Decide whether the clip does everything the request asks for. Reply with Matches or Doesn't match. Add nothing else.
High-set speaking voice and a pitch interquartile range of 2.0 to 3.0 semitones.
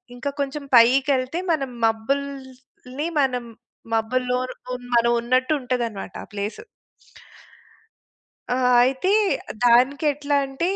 Matches